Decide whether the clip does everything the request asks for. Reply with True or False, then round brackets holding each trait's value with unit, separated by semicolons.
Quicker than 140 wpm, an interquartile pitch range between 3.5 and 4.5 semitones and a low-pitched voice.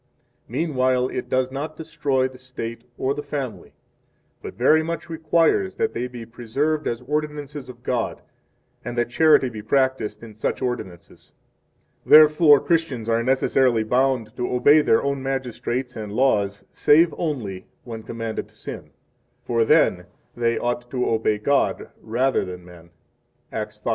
True (155 wpm; 4.0 semitones; 125 Hz)